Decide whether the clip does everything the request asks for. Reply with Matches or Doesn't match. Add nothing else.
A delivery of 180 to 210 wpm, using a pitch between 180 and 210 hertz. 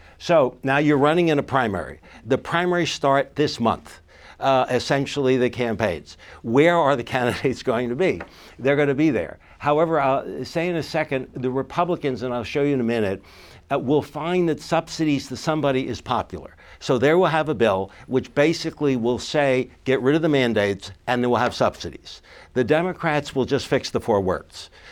Doesn't match